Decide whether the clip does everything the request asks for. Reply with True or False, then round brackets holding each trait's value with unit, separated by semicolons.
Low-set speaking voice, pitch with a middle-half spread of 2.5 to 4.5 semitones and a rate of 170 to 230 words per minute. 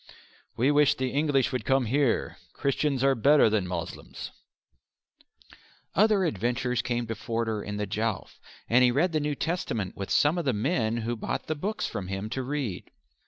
False (125 Hz; 4.9 semitones; 175 wpm)